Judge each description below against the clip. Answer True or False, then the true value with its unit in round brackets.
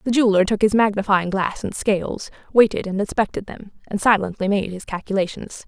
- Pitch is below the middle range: False (200 Hz)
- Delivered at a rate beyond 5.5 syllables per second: True (5.8 syllables/s)